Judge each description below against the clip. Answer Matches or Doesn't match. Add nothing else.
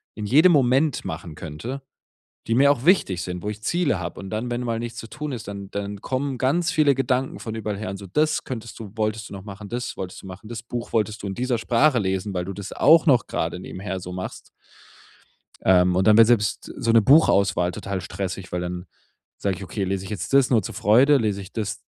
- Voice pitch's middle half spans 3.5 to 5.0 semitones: Matches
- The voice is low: Matches